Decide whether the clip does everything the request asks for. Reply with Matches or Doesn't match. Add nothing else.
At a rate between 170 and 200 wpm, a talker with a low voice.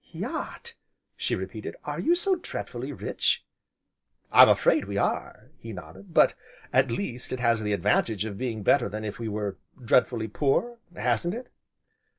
Doesn't match